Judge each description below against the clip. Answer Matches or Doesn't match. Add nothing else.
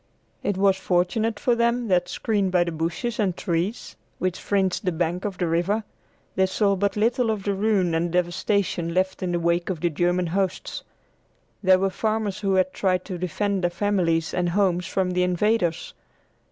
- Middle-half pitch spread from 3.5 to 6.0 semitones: Doesn't match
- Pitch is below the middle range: Doesn't match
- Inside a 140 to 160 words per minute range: Doesn't match